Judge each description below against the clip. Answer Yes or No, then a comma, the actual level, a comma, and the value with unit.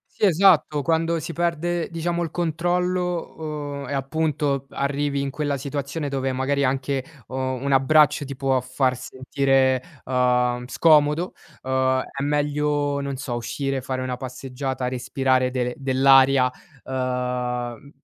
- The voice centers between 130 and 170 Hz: Yes, medium, 140 Hz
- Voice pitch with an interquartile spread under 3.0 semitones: Yes, narrow, 2.4 semitones